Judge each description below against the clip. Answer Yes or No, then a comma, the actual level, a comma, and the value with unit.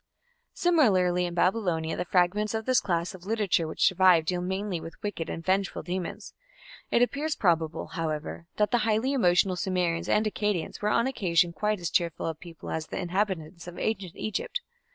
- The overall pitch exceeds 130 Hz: Yes, medium, 185 Hz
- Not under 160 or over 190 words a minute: Yes, average, 175 wpm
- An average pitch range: Yes, average, 3.7 semitones